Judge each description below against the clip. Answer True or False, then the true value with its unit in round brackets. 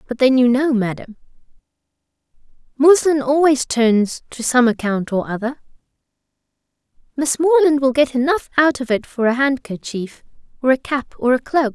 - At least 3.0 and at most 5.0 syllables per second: True (4.9 syllables/s)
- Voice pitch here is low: False (260 Hz)